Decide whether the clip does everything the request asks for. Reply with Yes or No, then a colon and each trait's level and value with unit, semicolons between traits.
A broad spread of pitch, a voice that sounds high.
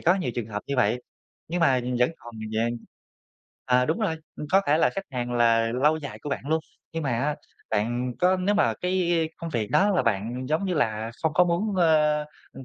No: wide, 6.2 semitones; medium, 150 Hz